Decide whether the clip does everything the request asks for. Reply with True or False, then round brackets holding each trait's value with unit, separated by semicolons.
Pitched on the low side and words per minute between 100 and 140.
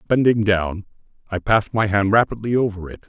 False (105 Hz; 175 wpm)